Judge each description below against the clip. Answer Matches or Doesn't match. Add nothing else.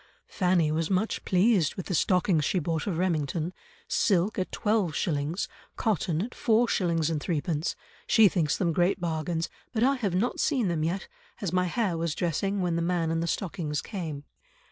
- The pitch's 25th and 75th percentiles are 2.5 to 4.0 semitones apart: Matches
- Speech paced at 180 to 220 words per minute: Matches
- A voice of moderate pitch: Matches